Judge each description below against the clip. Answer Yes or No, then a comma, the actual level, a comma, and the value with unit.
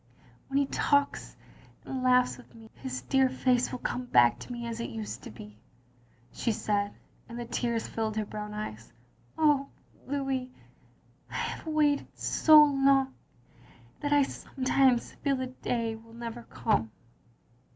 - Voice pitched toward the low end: No, high, 245 Hz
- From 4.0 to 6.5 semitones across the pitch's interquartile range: No, average, 3.6 semitones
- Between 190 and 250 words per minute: No, average, 160 wpm